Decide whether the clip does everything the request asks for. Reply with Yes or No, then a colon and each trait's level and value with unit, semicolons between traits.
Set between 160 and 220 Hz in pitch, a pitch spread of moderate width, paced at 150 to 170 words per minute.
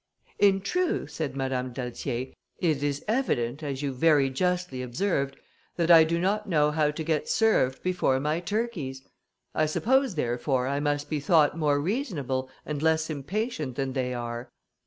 No: medium, 150 Hz; average, 4.9 semitones; average, 160 wpm